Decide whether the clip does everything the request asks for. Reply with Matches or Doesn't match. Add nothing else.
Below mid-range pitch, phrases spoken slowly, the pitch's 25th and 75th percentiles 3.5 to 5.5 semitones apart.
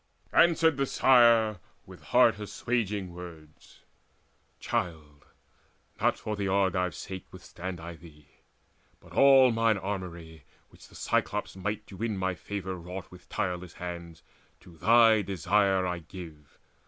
Matches